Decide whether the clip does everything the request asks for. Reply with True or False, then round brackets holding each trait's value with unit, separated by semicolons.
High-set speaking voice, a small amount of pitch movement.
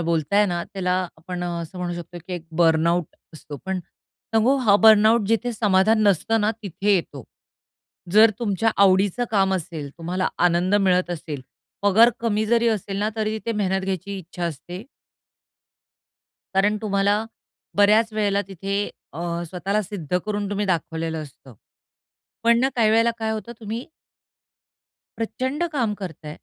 False (195 Hz; 3.7 semitones)